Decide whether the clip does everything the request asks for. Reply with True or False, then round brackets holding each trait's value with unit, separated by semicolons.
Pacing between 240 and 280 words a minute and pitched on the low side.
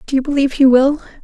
False (245 wpm; 270 Hz)